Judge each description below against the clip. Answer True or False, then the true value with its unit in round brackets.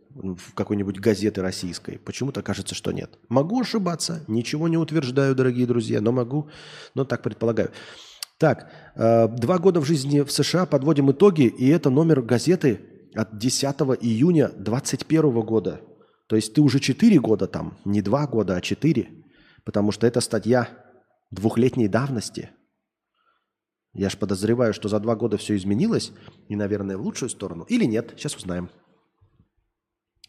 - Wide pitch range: False (5.0 semitones)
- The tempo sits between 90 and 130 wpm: False (145 wpm)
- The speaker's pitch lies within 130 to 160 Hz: False (115 Hz)